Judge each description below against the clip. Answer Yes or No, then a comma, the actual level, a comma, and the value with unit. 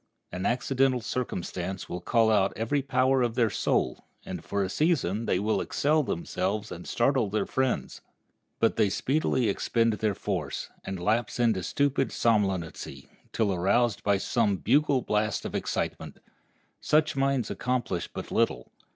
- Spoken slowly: No, average, 150 wpm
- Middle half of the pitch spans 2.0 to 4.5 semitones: No, average, 4.9 semitones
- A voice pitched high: No, low, 110 Hz